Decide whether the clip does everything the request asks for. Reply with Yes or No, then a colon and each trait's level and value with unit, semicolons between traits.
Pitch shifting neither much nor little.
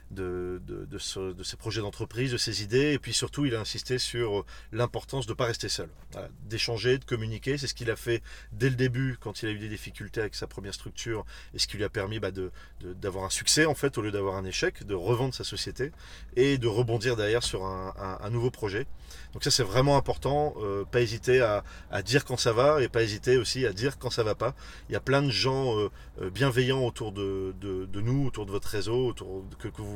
Yes: average, 4.3 semitones